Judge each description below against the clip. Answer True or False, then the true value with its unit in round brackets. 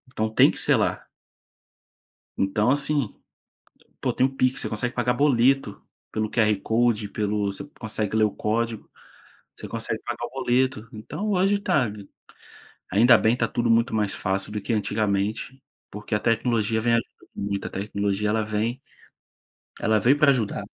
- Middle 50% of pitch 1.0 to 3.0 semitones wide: True (2.7 semitones)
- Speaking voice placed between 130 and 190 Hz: False (110 Hz)